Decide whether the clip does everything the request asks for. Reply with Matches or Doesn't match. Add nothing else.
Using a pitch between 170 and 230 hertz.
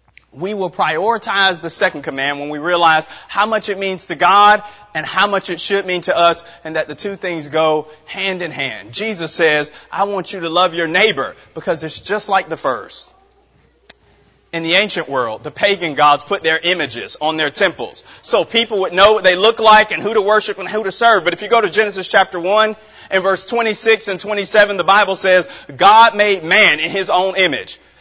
Matches